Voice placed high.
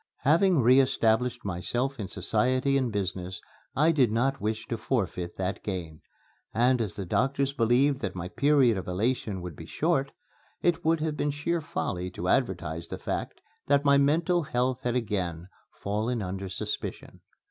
No: low, 120 Hz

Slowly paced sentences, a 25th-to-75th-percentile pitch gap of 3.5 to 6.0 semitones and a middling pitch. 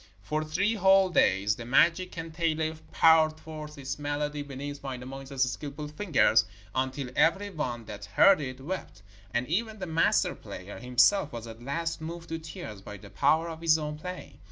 No: average, 170 wpm; average, 4.4 semitones; medium, 150 Hz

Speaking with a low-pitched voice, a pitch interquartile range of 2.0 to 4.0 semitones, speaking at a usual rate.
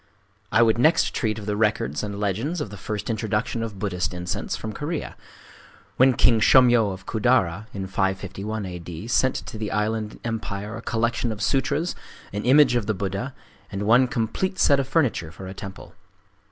Yes: low, 110 Hz; average, 3.7 semitones; average, 180 wpm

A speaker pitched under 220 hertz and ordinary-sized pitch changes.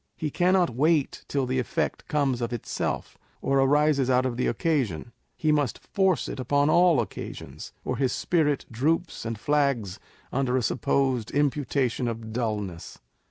Yes: low, 135 Hz; average, 3.8 semitones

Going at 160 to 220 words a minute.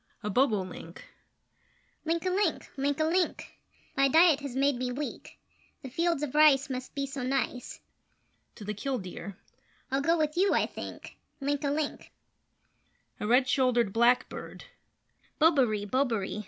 No: average, 145 wpm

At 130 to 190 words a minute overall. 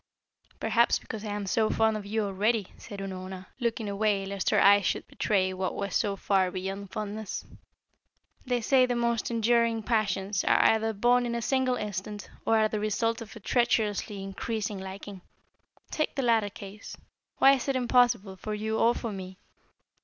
Yes: average, 180 wpm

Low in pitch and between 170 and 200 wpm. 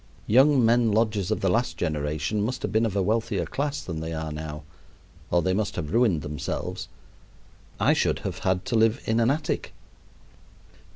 Yes: low, 105 Hz; average, 180 wpm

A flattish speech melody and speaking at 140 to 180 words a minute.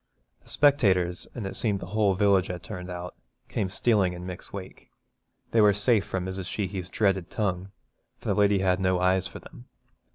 No: narrow, 2.1 semitones; average, 190 wpm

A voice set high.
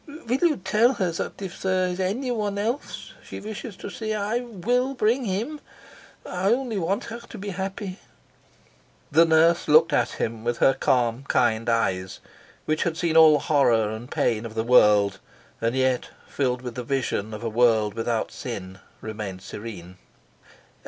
No: medium, 160 Hz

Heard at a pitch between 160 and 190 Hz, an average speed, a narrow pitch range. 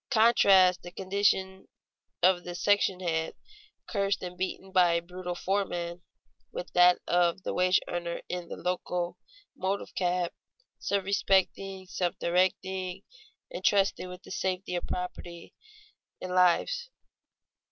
No: medium, 185 Hz; slow, 125 wpm; narrow, 1.5 semitones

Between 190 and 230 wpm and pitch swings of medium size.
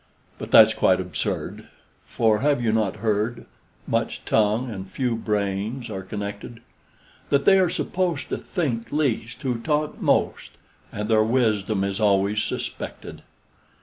No: average, 140 wpm; average, 3.8 semitones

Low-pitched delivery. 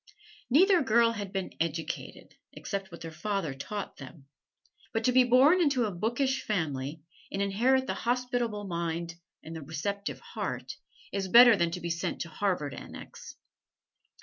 No: high, 200 Hz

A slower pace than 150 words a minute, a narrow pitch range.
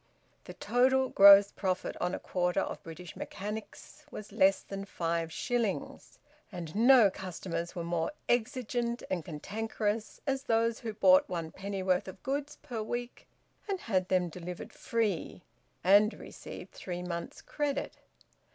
No: average, 140 wpm; average, 4.6 semitones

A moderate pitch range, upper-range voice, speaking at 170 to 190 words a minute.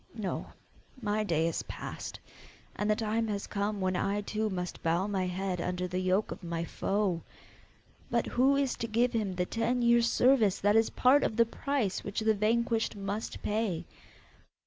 Yes: average, 3.5 semitones; high, 210 Hz; average, 180 wpm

